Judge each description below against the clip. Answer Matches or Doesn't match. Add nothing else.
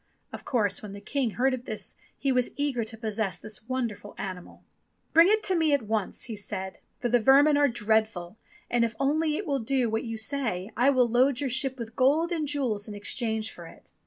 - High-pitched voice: Matches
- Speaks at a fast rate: Matches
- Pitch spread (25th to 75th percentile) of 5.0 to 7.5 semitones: Doesn't match